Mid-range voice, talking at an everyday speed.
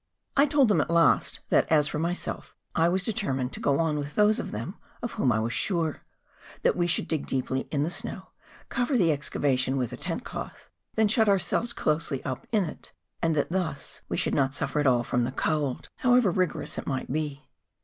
No: medium, 155 Hz; fast, 220 wpm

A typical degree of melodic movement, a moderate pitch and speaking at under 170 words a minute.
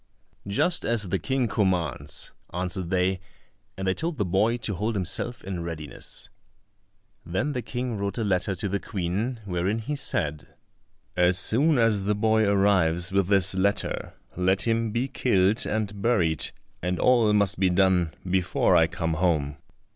No: average, 3.7 semitones; very low, 95 Hz; average, 160 wpm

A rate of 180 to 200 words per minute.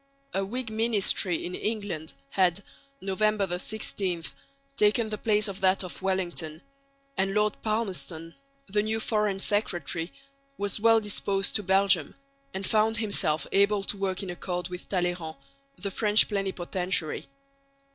No: slow, 135 wpm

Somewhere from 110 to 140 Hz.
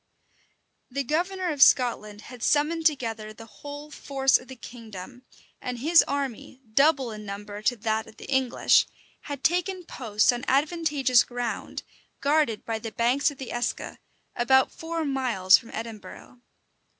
No: very high, 255 Hz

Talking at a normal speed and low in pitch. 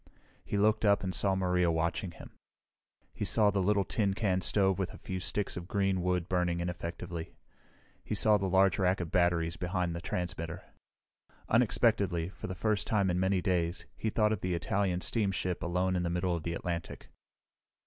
Yes: average, 185 wpm; very low, 90 Hz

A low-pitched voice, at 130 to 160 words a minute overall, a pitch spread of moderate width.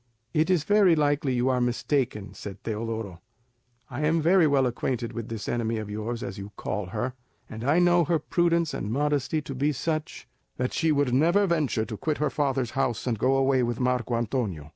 No: low, 130 Hz; average, 200 wpm; average, 4.8 semitones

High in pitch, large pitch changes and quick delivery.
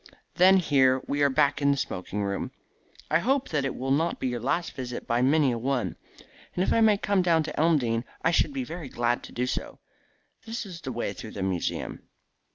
No: medium, 140 Hz; wide, 5.7 semitones; fast, 220 wpm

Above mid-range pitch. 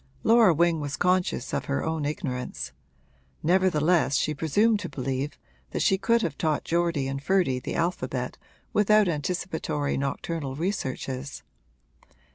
No: medium, 160 Hz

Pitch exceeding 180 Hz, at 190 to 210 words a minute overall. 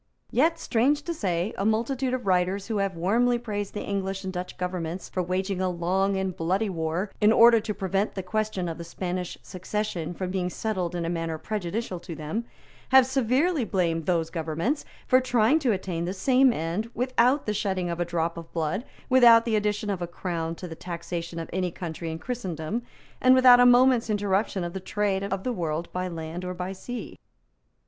Yes: high, 190 Hz; average, 200 wpm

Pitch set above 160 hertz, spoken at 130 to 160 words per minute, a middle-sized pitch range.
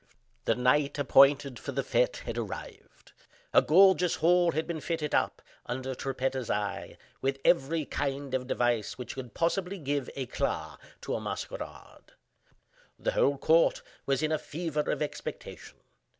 No: medium, 140 Hz; average, 150 wpm; average, 4.0 semitones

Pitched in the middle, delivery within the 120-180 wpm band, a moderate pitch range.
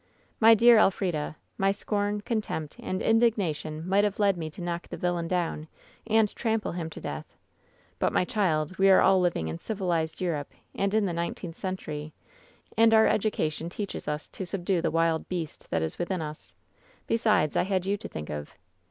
No: medium, 180 Hz; average, 190 wpm; average, 4.3 semitones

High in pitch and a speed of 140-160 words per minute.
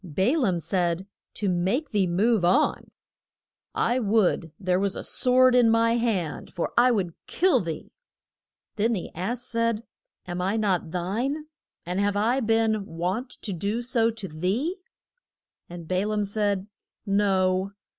Yes: high, 205 Hz; average, 150 wpm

